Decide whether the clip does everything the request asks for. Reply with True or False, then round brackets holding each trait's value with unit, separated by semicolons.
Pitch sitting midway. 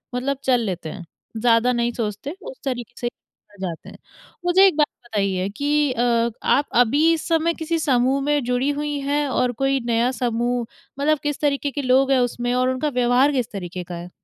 False (255 Hz)